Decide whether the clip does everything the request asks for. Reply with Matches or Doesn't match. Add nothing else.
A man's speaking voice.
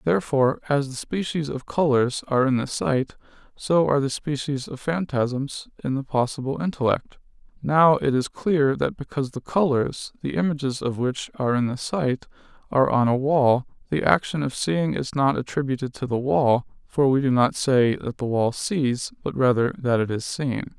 Matches